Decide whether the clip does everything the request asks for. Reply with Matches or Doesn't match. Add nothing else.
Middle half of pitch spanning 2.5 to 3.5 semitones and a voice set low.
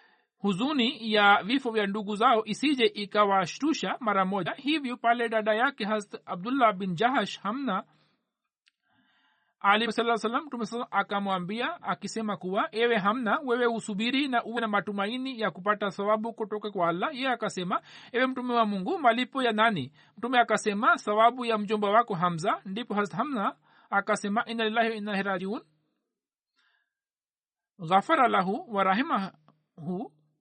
Doesn't match